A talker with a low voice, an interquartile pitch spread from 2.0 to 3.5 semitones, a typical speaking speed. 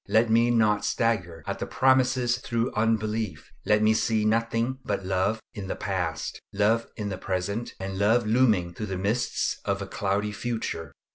Yes: low, 110 Hz; average, 2.9 semitones; average, 170 wpm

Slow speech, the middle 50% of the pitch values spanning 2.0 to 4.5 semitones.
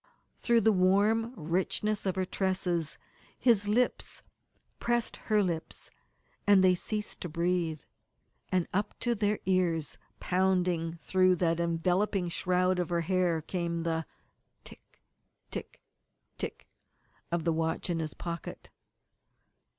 Yes: slow, 125 wpm; average, 2.9 semitones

